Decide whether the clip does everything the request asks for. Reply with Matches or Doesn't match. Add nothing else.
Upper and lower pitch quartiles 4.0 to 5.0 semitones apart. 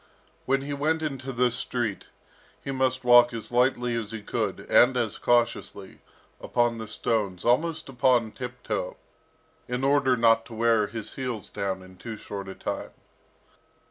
Doesn't match